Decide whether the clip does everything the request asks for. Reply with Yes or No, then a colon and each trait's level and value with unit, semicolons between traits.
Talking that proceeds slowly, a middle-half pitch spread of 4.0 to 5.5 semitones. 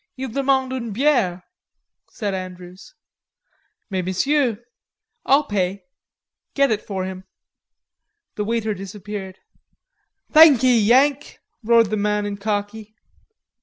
Yes: slow, 105 wpm; average, 4.8 semitones